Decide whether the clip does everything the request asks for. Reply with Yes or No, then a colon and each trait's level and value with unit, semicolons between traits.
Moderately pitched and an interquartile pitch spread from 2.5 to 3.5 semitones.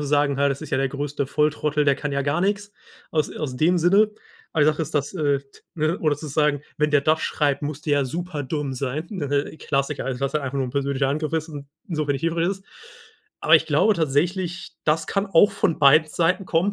Yes: medium, 150 Hz; average, 2.8 semitones